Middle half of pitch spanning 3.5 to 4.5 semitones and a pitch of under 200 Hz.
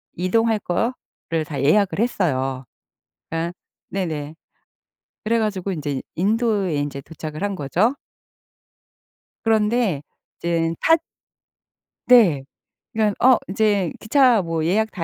No: wide, 5.6 semitones; high, 190 Hz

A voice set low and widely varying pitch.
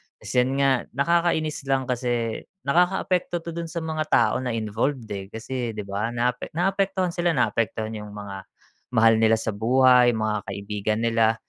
Yes: low, 125 Hz; wide, 6.1 semitones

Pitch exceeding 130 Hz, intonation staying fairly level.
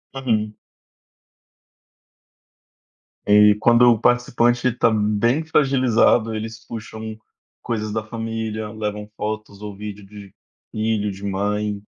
No: low, 110 Hz; narrow, 1.9 semitones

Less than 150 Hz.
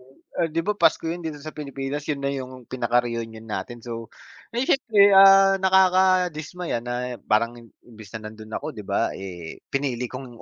Yes: low, 135 Hz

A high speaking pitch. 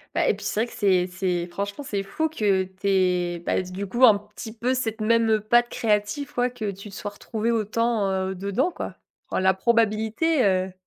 Yes: high, 210 Hz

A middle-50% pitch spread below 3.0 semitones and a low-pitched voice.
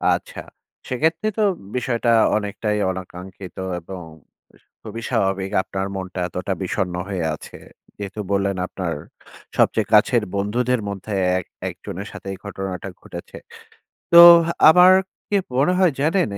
No: average, 4.8 semitones; low, 100 Hz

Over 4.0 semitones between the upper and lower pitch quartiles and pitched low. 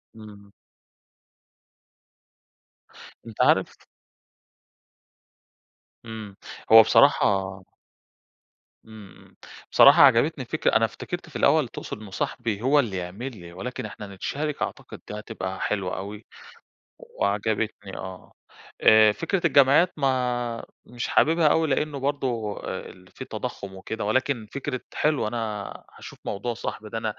Yes: average, 4.6 semitones; low, 110 Hz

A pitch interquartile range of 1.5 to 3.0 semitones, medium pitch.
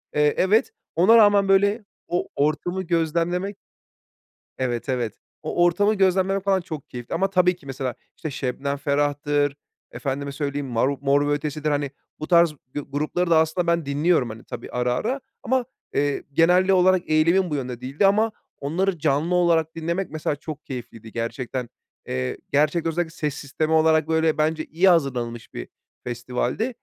No: average, 4.3 semitones; medium, 155 Hz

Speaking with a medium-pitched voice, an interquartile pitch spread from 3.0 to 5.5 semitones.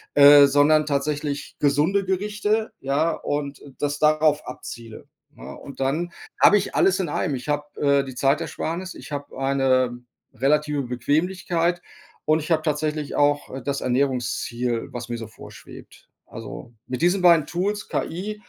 Yes: medium, 145 Hz; average, 3.6 semitones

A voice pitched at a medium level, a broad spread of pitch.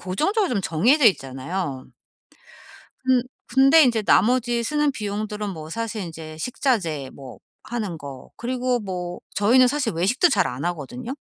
No: high, 210 Hz; wide, 7.2 semitones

